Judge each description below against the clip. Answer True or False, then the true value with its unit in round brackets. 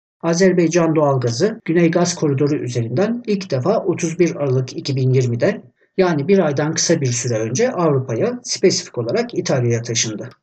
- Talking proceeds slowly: False (130 wpm)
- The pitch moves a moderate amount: False (5.9 semitones)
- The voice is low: False (165 Hz)